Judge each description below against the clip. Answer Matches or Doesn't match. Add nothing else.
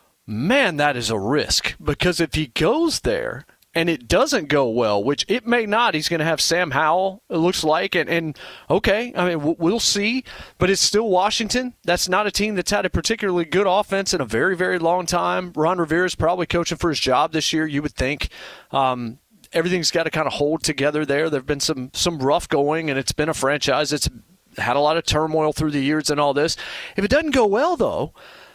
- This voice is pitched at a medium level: Matches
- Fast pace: Matches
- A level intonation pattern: Doesn't match